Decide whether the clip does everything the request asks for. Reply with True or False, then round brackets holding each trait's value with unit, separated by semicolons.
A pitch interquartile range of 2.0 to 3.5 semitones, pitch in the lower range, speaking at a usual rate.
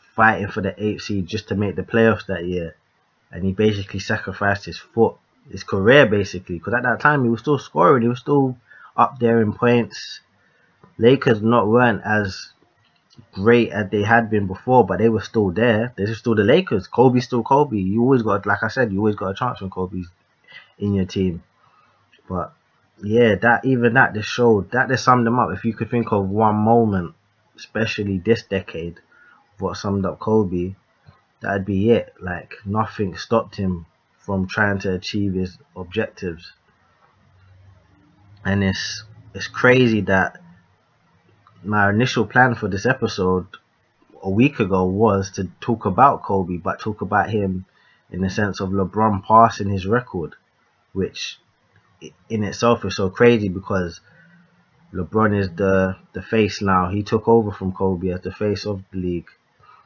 True (3.2 semitones; 105 Hz; 170 wpm)